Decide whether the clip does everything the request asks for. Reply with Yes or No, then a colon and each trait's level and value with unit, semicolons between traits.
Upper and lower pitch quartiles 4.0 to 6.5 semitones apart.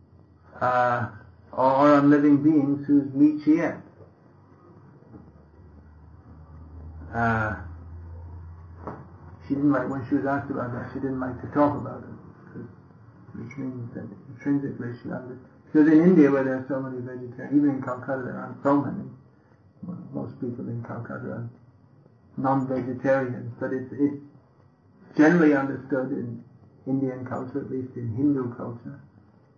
Yes: average, 4.7 semitones